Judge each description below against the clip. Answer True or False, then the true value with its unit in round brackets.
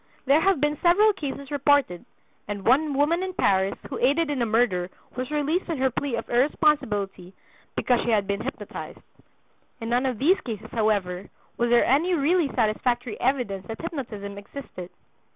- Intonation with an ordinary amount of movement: False (5.7 semitones)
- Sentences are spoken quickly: False (170 wpm)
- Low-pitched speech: False (255 Hz)